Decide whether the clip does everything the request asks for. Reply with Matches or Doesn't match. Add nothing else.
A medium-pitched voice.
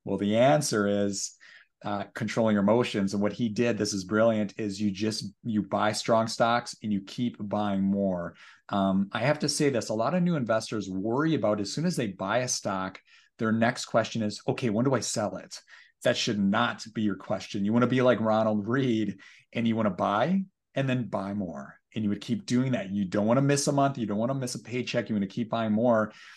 Doesn't match